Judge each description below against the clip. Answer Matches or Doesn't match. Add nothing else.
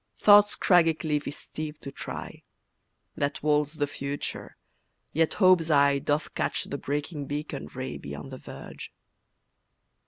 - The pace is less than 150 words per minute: Matches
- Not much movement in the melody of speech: Matches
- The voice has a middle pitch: Matches